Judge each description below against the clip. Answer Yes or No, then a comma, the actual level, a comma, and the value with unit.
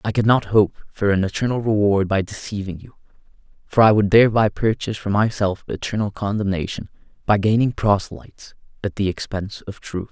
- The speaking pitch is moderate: No, low, 105 Hz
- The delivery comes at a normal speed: Yes, average, 165 wpm